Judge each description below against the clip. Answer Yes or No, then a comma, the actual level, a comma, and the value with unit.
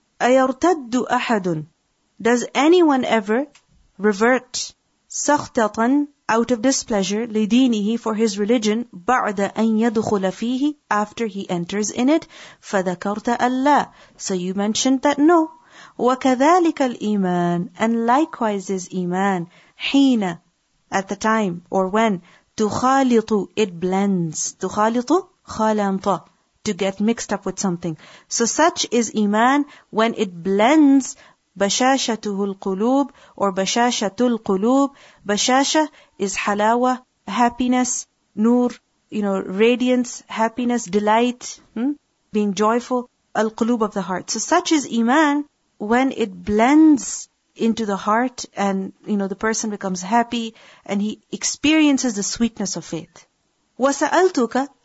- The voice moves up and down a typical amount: Yes, average, 4.1 semitones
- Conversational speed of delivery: No, slow, 115 wpm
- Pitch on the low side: No, high, 225 Hz